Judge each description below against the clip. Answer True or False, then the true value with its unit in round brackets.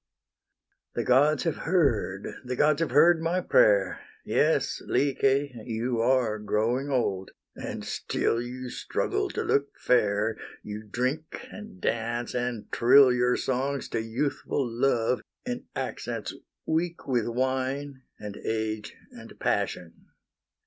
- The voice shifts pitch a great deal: False (4.0 semitones)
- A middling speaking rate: False (125 wpm)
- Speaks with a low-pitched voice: True (125 Hz)